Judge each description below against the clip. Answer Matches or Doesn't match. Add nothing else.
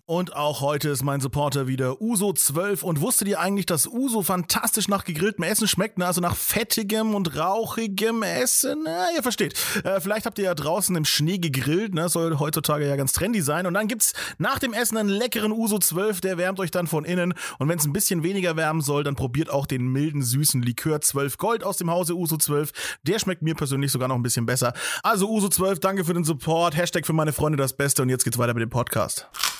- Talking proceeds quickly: Matches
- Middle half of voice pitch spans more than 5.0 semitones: Matches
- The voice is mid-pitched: Matches